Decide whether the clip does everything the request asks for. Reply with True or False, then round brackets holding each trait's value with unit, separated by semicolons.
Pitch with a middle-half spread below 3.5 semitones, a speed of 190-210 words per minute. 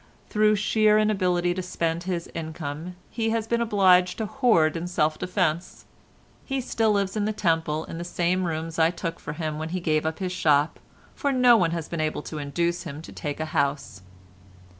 False (4.4 semitones; 200 wpm)